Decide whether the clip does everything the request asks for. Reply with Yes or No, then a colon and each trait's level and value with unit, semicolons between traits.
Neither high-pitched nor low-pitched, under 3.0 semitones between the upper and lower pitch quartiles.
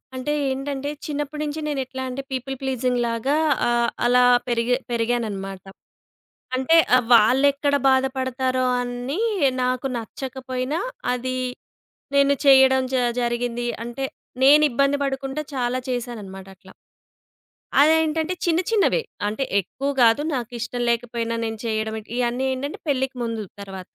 No: very high, 255 Hz; narrow, 2.6 semitones